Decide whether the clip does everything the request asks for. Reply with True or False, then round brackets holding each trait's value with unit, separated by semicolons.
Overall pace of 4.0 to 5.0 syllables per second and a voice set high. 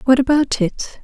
True (4.9 syllables/s; 260 Hz)